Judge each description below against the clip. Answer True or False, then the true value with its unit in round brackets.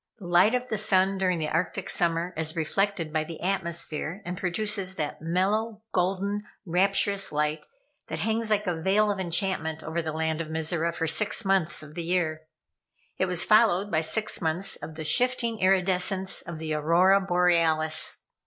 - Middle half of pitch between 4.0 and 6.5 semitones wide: False (3.6 semitones)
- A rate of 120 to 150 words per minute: False (170 wpm)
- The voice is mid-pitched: True (180 Hz)